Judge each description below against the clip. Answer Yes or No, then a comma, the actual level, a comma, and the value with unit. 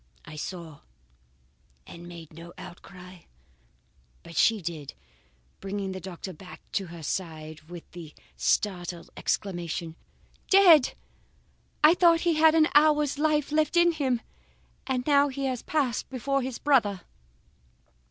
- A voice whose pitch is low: No, high, 205 Hz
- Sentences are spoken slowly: Yes, slow, 125 wpm